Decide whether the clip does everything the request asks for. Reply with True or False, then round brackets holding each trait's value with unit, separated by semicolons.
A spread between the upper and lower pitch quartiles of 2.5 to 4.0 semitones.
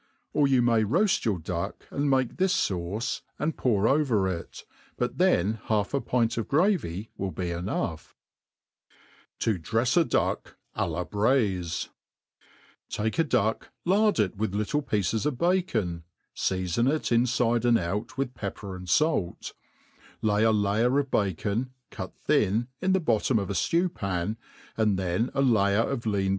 False (5.4 semitones)